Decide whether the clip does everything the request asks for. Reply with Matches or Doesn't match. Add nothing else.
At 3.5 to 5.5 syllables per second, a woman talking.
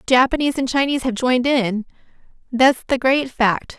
Doesn't match